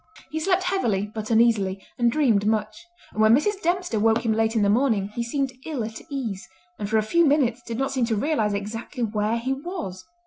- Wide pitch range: No, average, 4.5 semitones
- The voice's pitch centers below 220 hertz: No, high, 230 Hz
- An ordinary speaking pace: No, fast, 215 wpm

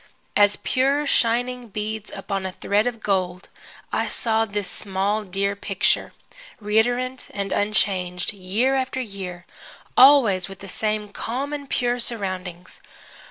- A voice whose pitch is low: No, high, 210 Hz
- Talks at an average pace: No, slow, 130 wpm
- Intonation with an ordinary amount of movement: Yes, average, 3.9 semitones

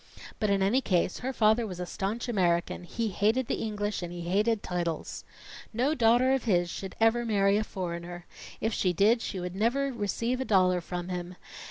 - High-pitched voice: Yes, high, 205 Hz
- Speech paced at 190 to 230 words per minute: Yes, average, 195 wpm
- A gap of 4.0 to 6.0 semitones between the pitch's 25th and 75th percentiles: Yes, average, 4.4 semitones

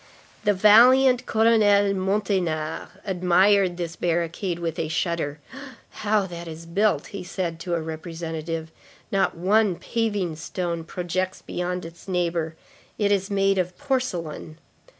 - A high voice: No, medium, 180 Hz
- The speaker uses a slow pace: Yes, slow, 125 wpm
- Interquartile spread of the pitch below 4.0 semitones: Yes, average, 3.5 semitones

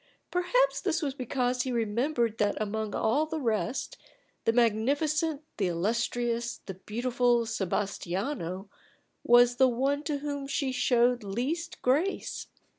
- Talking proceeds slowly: Yes, slow, 125 wpm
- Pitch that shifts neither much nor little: Yes, average, 4.4 semitones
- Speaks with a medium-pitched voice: No, high, 245 Hz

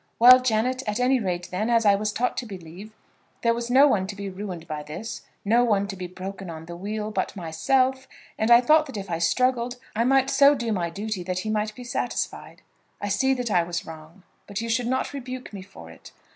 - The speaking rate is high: Yes, fast, 230 wpm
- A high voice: Yes, high, 215 Hz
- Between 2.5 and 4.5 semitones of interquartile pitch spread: No, average, 5.0 semitones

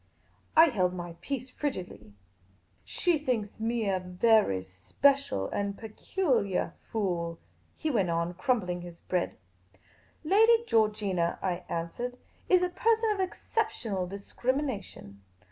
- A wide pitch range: Yes, wide, 7.9 semitones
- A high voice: Yes, high, 210 Hz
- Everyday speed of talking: No, slow, 130 wpm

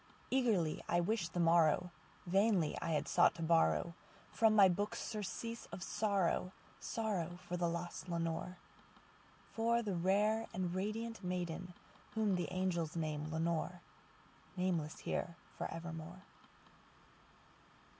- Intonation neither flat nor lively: Yes, average, 3.5 semitones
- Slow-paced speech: Yes, slow, 105 wpm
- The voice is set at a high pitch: No, medium, 180 Hz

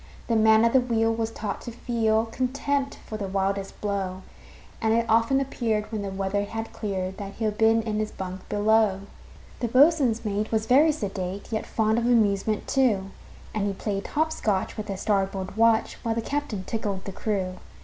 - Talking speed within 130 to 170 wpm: No, average, 190 wpm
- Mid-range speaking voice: No, high, 220 Hz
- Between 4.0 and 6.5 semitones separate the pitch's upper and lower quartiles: No, narrow, 2.6 semitones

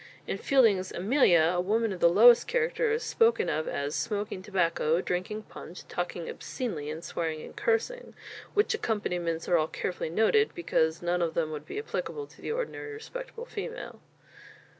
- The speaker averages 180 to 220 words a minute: No, average, 165 wpm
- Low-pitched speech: No, high, 195 Hz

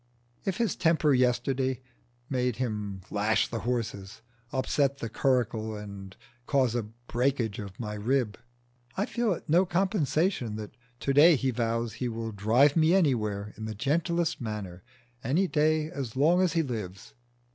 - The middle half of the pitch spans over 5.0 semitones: Yes, wide, 5.6 semitones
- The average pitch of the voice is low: Yes, low, 125 Hz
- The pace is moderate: Yes, average, 155 wpm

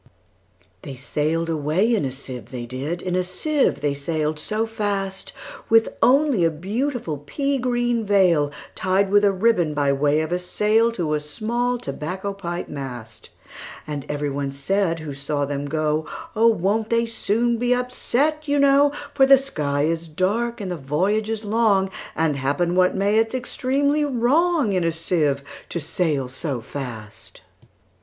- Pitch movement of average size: No, wide, 7.6 semitones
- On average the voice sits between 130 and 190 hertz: Yes, medium, 185 Hz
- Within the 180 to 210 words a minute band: No, average, 150 wpm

